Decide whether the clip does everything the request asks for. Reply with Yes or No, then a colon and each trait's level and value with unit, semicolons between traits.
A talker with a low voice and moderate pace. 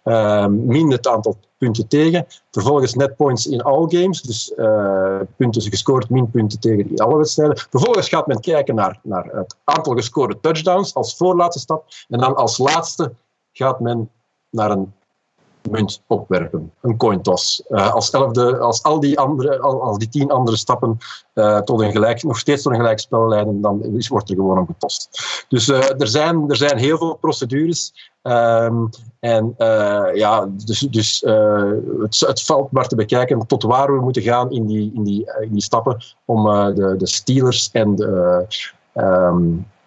Yes: low, 120 Hz; average, 175 wpm